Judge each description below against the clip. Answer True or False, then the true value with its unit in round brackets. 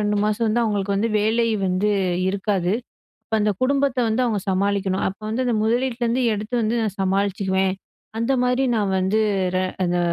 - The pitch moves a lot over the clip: False (3.2 semitones)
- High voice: True (210 Hz)